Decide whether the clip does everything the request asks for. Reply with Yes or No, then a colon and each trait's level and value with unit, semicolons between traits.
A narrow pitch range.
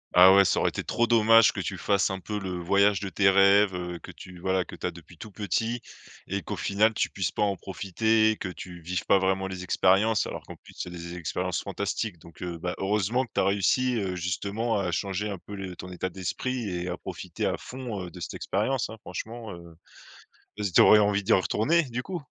No: average, 3.2 semitones